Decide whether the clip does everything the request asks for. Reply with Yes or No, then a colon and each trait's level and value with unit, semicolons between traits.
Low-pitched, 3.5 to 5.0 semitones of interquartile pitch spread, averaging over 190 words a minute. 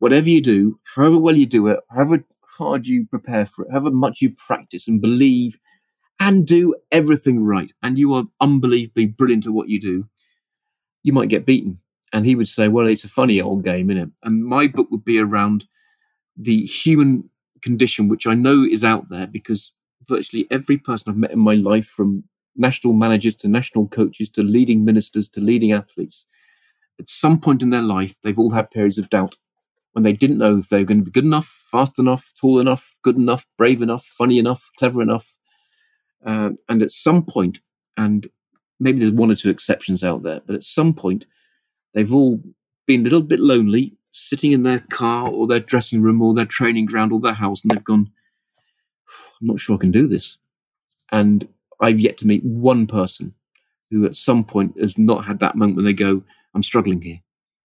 Yes: low, 115 Hz; average, 4.2 semitones; average, 200 wpm